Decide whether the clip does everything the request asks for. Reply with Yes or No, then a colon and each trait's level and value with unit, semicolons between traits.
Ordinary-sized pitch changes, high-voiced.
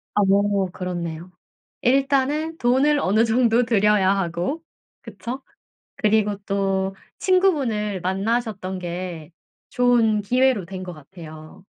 Yes: average, 4.9 semitones; high, 210 Hz